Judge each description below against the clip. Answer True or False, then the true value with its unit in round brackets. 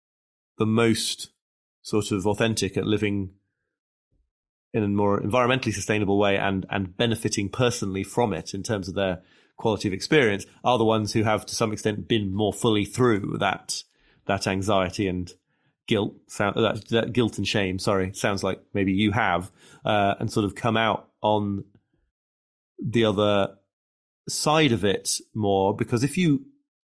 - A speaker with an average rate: True (155 wpm)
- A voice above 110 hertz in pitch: False (105 Hz)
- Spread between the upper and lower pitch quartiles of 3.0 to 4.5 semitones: False (2.6 semitones)